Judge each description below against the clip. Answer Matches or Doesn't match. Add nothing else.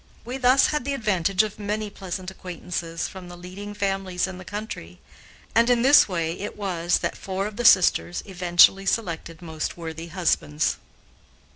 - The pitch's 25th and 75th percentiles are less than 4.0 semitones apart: Matches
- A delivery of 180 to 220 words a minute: Doesn't match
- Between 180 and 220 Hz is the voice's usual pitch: Matches